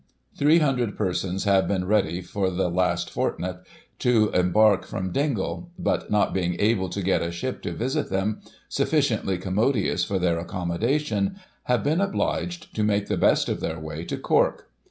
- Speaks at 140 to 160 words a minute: No, average, 170 wpm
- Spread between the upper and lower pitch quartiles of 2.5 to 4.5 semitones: No, average, 5.3 semitones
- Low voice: Yes, low, 100 Hz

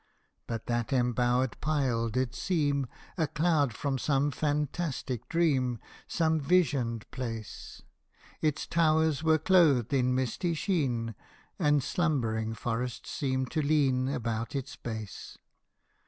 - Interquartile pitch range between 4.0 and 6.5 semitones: Yes, average, 4.3 semitones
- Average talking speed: No, slow, 115 wpm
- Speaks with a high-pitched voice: No, low, 135 Hz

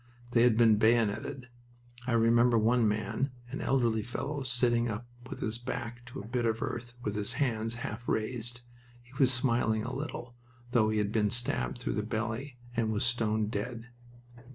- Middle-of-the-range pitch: No, low, 115 Hz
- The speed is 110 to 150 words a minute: No, average, 175 wpm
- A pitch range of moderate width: No, narrow, 2.0 semitones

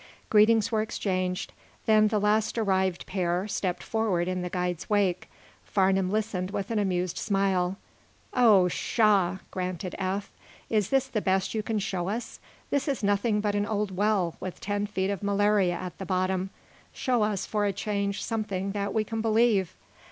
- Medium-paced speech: Yes, average, 170 wpm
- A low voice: No, high, 200 Hz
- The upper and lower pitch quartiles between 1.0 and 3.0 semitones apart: Yes, narrow, 2.5 semitones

